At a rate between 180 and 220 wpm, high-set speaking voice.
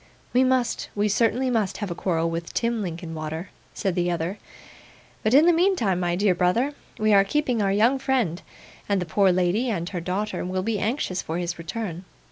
Yes: average, 195 wpm; high, 195 Hz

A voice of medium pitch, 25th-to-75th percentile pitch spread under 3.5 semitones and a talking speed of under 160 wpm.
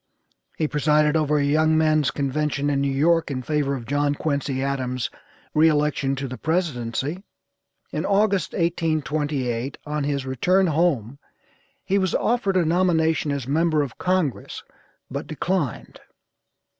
Yes: medium, 150 Hz; average, 2.8 semitones; average, 140 wpm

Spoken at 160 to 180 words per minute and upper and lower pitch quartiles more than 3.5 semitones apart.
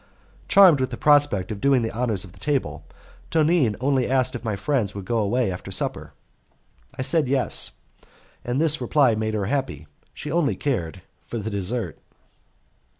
Yes: average, 175 wpm; average, 5.0 semitones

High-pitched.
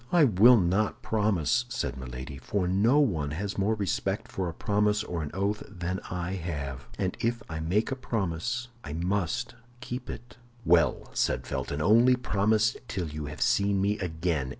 No: very low, 95 Hz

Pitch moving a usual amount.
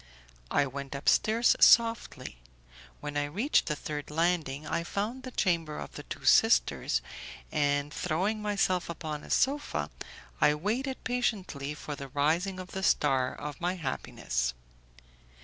No: wide, 5.9 semitones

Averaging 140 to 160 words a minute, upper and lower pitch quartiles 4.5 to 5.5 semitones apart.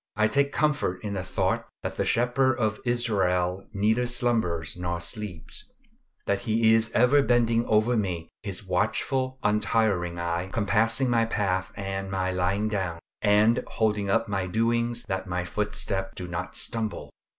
No: average, 150 wpm; average, 3.8 semitones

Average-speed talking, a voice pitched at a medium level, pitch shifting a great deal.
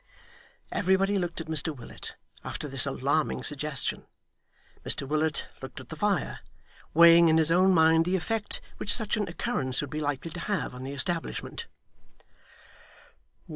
No: average, 150 wpm; medium, 160 Hz; average, 4.0 semitones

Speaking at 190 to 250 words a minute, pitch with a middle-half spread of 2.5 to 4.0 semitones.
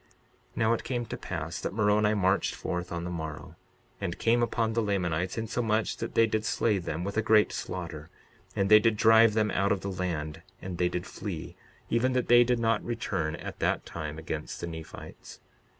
No: average, 200 wpm; average, 4.6 semitones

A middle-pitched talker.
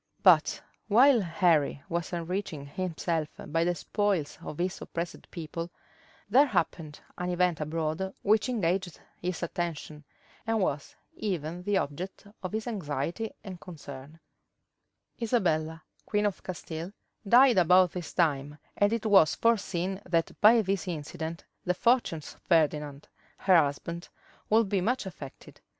Yes: medium, 175 Hz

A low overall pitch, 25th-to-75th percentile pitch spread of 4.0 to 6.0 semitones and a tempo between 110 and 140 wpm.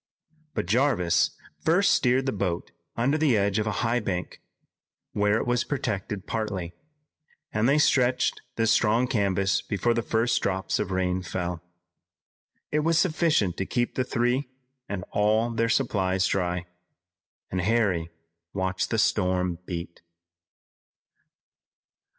Yes: low, 105 Hz; average, 4.7 semitones; slow, 135 wpm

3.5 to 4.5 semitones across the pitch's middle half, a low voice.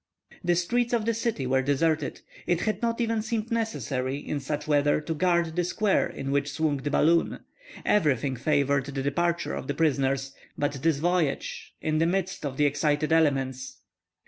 No: average, 4.1 semitones; medium, 155 Hz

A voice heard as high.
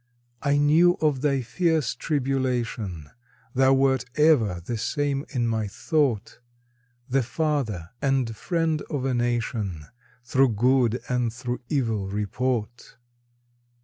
No: low, 125 Hz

